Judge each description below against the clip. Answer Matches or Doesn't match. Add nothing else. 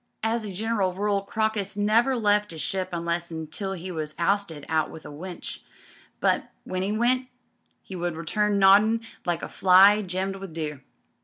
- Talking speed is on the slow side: Doesn't match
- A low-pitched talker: Doesn't match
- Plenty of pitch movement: Doesn't match